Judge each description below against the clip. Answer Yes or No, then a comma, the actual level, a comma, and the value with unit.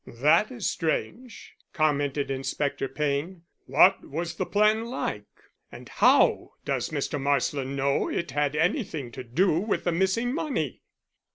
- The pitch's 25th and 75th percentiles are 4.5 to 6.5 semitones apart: Yes, wide, 5.5 semitones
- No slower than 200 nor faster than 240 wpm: No, average, 140 wpm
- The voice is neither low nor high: Yes, medium, 155 Hz